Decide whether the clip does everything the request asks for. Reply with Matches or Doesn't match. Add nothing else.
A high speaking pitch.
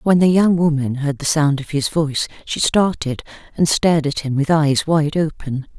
Doesn't match